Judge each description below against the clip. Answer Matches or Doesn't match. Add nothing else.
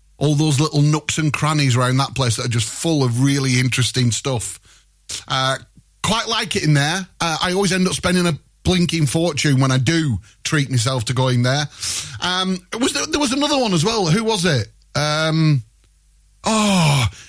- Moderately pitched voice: Matches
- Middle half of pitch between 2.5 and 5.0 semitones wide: Doesn't match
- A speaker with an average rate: Matches